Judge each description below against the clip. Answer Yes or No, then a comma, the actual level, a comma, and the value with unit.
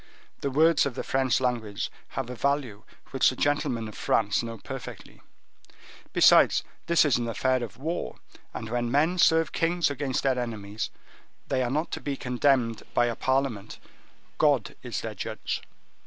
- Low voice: Yes, low, 130 Hz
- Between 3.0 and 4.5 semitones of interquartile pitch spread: Yes, average, 3.5 semitones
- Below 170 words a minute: Yes, average, 160 wpm